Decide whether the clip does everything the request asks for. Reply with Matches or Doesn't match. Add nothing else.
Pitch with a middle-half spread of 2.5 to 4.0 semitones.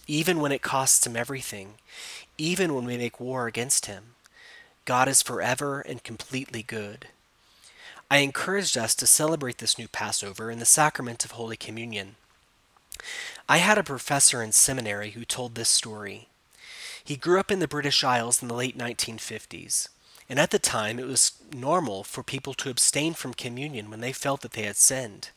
Matches